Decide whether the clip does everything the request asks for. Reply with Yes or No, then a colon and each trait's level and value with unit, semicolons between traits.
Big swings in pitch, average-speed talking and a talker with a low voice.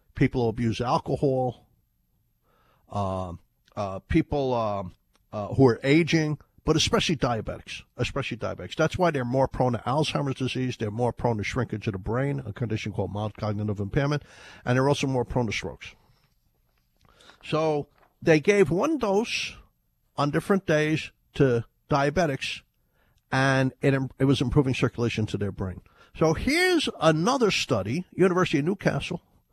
Yes: wide, 6.2 semitones; average, 145 wpm; low, 130 Hz